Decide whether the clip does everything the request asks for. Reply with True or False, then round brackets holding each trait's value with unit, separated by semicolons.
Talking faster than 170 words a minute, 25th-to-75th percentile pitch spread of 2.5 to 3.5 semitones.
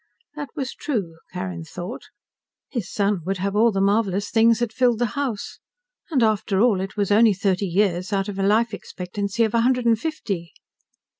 True (190 wpm; 3.2 semitones)